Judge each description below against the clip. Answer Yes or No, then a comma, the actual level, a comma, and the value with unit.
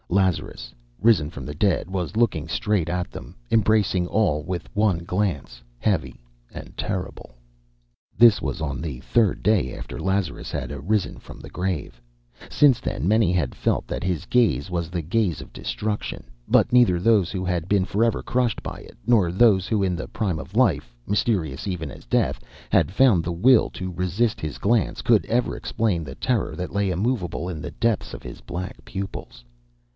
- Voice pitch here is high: No, very low, 95 Hz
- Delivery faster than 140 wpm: Yes, average, 180 wpm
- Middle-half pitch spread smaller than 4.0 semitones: No, average, 4.3 semitones